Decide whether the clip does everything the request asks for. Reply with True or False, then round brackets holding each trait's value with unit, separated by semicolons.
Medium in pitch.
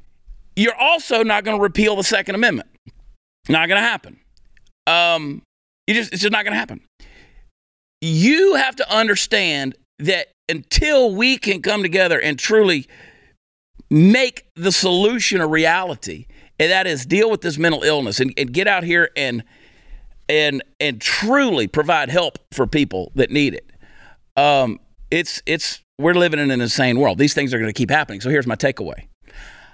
True (170 Hz)